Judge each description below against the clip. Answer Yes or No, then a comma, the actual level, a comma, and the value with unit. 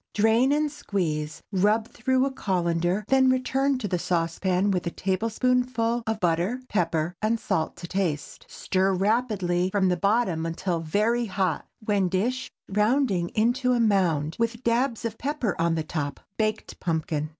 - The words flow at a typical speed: Yes, average, 155 wpm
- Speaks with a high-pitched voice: Yes, high, 200 Hz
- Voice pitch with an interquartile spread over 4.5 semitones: Yes, average, 5.2 semitones